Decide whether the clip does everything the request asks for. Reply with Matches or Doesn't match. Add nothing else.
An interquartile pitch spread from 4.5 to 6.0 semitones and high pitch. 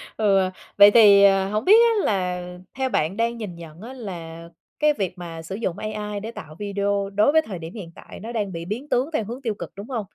Doesn't match